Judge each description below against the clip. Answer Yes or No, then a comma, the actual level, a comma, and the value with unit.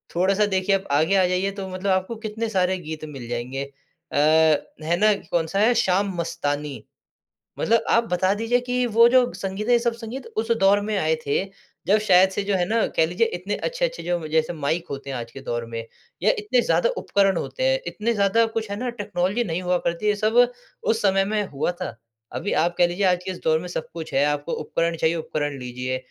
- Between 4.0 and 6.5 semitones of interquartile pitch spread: Yes, average, 5.1 semitones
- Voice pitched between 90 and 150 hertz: No, medium, 185 Hz